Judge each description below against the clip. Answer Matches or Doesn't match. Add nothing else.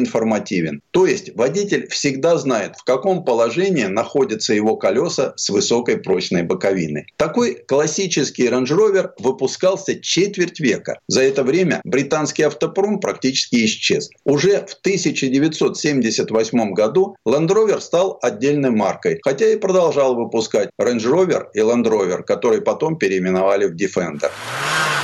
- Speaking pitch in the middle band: Matches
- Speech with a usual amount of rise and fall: Doesn't match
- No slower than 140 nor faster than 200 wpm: Doesn't match